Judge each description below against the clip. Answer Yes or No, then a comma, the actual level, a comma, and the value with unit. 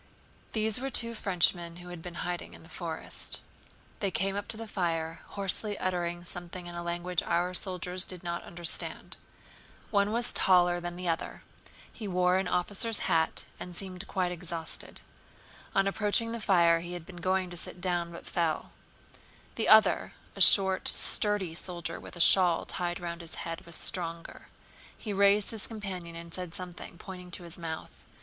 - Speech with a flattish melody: Yes, narrow, 2.2 semitones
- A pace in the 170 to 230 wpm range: Yes, average, 175 wpm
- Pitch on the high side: No, medium, 180 Hz